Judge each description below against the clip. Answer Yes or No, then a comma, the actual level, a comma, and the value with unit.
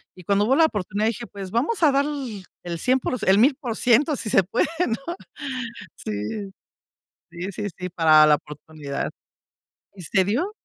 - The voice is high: Yes, high, 210 Hz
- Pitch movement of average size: No, wide, 6.3 semitones